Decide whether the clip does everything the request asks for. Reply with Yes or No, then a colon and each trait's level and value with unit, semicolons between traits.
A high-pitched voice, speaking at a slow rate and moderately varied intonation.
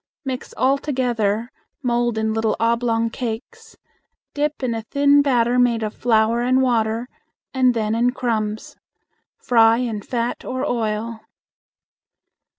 No: high, 235 Hz; slow, 130 wpm; narrow, 2.2 semitones